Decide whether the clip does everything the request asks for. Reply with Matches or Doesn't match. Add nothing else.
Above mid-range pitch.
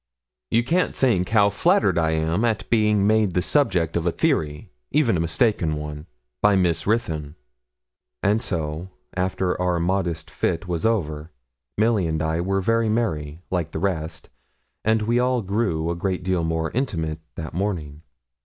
Doesn't match